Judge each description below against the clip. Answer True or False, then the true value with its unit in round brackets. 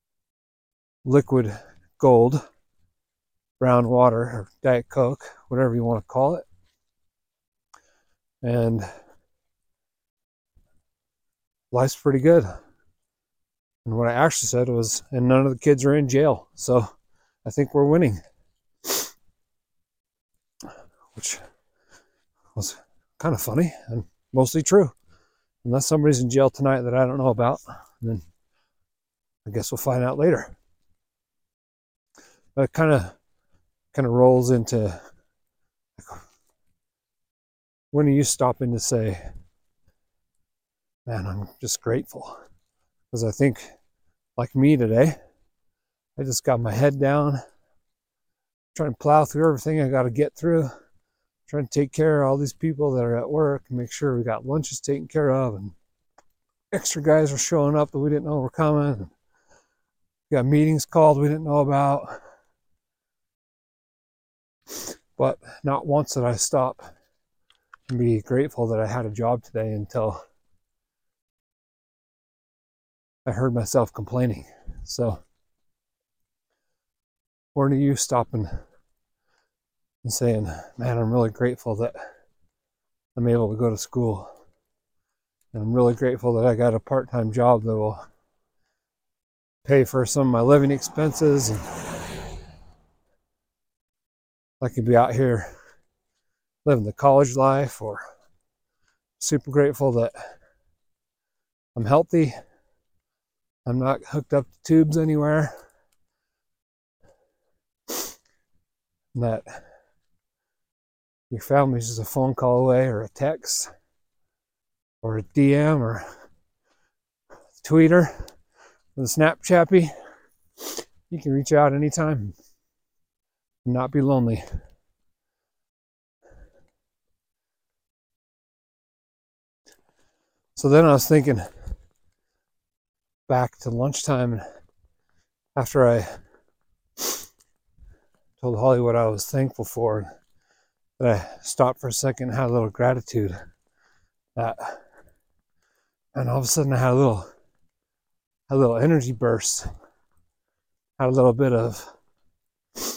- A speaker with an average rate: False (115 wpm)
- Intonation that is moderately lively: False (7.0 semitones)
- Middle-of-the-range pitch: False (120 Hz)